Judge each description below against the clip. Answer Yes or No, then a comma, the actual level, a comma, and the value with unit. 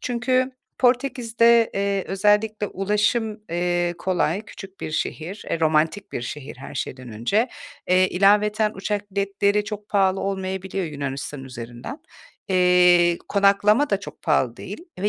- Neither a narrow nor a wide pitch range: Yes, average, 3.4 semitones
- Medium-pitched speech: No, high, 195 Hz